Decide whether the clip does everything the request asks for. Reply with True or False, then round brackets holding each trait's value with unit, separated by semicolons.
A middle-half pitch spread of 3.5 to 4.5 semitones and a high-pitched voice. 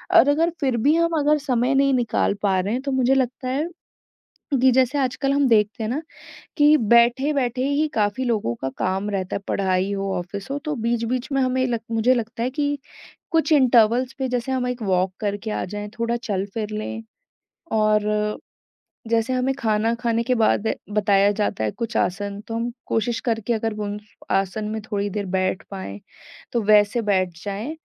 True (4.0 semitones; 230 Hz)